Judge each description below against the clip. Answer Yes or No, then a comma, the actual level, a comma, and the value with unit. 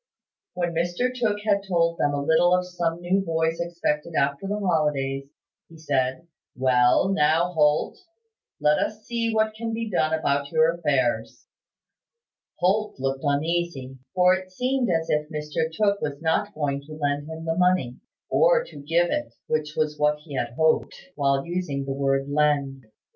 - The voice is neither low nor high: Yes, medium, 160 Hz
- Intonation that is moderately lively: Yes, average, 4.2 semitones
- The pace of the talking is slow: No, average, 165 wpm